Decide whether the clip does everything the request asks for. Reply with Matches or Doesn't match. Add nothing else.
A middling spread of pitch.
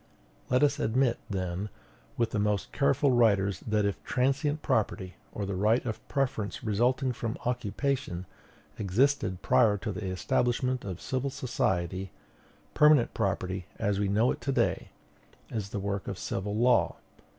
Matches